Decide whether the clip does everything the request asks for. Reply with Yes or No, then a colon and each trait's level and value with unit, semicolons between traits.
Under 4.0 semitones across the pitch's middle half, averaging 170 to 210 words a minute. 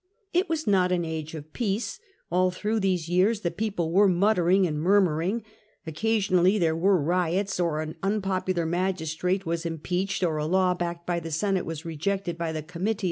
Yes: average, 2.9 semitones; average, 185 wpm